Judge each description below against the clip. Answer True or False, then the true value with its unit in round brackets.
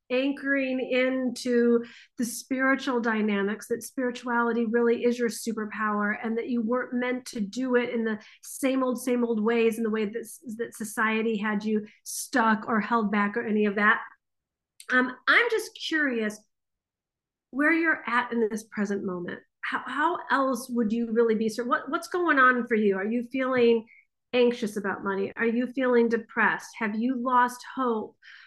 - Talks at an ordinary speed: True (170 wpm)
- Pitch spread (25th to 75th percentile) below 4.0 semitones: True (2.4 semitones)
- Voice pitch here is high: True (235 Hz)